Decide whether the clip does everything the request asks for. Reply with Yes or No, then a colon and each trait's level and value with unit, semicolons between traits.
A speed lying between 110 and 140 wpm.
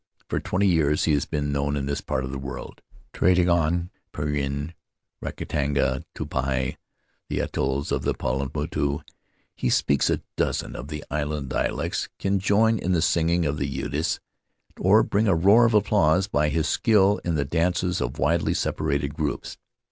No: average, 170 wpm